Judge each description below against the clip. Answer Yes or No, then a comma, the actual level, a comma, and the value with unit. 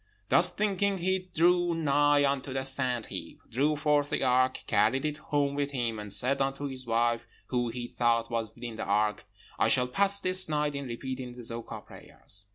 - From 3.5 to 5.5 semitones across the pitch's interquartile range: Yes, average, 3.9 semitones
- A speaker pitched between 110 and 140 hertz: Yes, low, 135 Hz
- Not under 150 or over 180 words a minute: No, average, 190 wpm